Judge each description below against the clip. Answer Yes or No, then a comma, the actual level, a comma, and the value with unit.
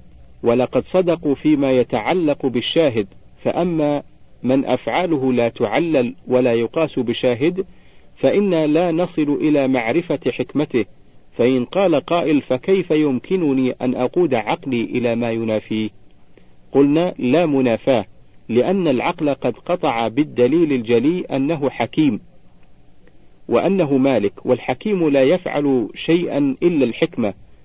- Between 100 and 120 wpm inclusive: Yes, average, 105 wpm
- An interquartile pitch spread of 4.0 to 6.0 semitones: Yes, average, 4.9 semitones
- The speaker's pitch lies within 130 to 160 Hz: Yes, low, 135 Hz